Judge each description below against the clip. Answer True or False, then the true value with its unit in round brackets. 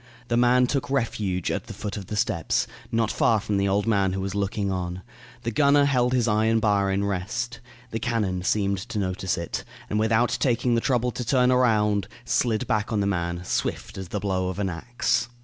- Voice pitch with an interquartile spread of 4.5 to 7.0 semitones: False (3.7 semitones)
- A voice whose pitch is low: True (105 Hz)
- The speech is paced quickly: True (210 wpm)